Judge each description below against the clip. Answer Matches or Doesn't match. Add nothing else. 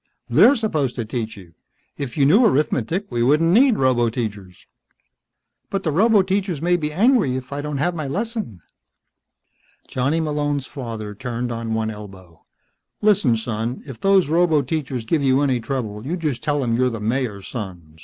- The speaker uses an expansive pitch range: Matches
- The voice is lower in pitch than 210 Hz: Matches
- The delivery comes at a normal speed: Matches